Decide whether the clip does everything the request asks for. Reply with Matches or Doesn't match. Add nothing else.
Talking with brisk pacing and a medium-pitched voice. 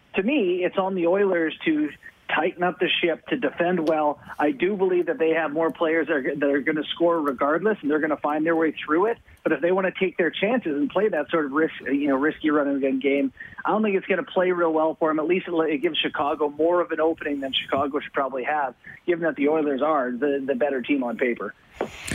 Matches